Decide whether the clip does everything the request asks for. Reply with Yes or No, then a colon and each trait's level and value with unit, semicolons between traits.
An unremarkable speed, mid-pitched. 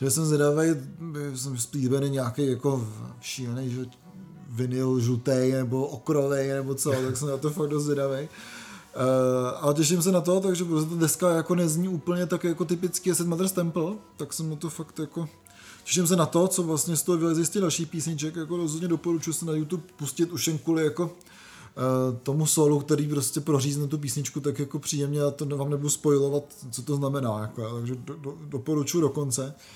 No: fast, 190 wpm; medium, 150 Hz